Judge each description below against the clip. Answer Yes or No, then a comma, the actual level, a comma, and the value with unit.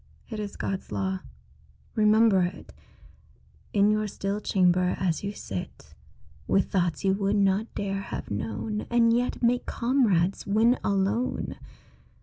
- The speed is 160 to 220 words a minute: No, slow, 135 wpm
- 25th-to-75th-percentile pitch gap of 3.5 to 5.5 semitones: No, narrow, 2.4 semitones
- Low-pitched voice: No, high, 200 Hz